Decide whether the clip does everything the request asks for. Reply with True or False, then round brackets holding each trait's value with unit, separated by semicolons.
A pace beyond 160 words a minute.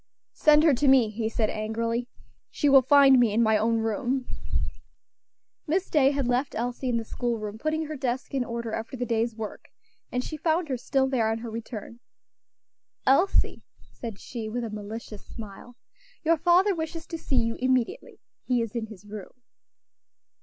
True (180 wpm)